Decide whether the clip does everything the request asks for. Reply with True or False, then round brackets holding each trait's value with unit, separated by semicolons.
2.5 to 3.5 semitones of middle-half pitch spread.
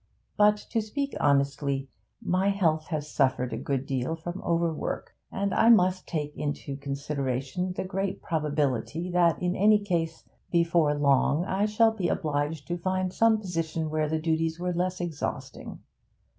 False (4.1 semitones)